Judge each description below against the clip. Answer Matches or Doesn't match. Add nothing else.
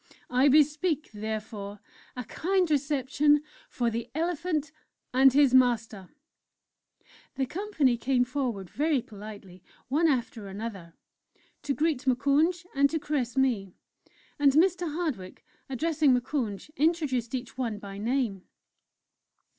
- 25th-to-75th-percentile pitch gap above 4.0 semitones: Matches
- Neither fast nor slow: Doesn't match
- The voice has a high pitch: Matches